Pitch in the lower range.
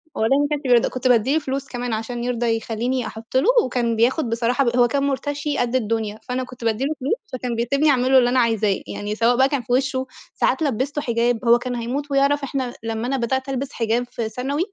No: very high, 250 Hz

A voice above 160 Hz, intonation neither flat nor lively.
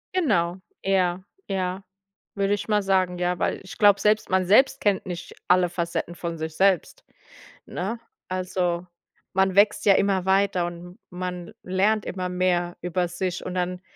No: medium, 185 Hz; narrow, 1.8 semitones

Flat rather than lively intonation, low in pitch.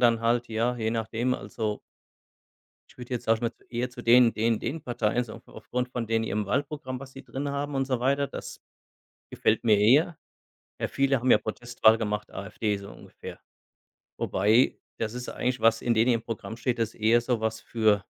Yes: narrow, 2.2 semitones; low, 115 Hz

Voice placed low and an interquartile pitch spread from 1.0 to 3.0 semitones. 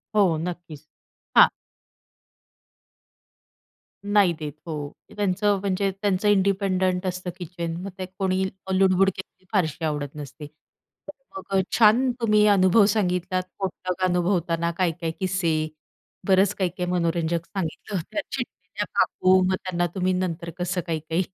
No: medium, 185 Hz; narrow, 2.4 semitones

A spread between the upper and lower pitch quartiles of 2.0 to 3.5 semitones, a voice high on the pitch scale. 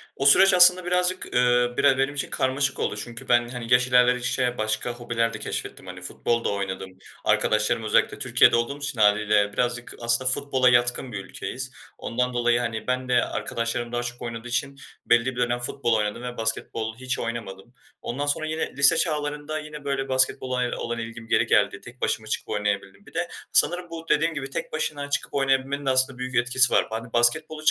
No: average, 2.9 semitones; low, 125 Hz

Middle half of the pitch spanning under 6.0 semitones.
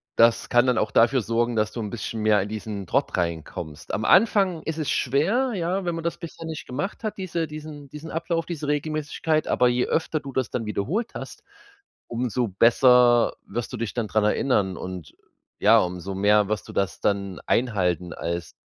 No: wide, 7.1 semitones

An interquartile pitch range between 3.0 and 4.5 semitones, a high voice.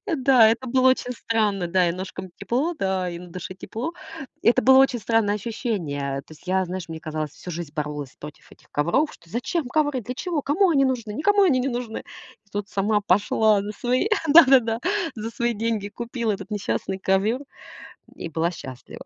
No: wide, 5.6 semitones; high, 215 Hz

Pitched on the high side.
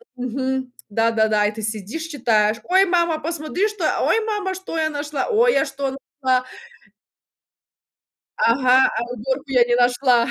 Yes: very high, 265 Hz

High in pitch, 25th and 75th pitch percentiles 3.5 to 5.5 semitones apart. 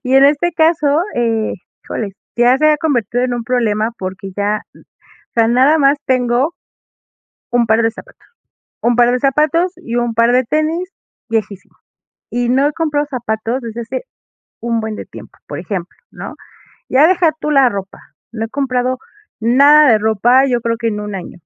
Yes: high, 245 Hz; average, 4.1 semitones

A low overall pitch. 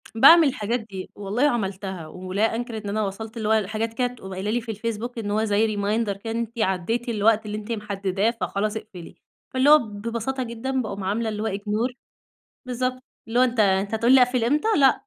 No: high, 220 Hz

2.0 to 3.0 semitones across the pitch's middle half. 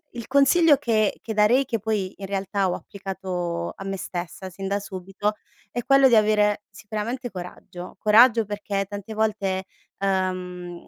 Yes: average, 2.7 semitones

